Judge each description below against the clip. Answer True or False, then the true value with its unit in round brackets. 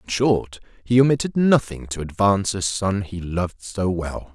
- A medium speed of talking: True (180 wpm)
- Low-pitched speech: True (100 Hz)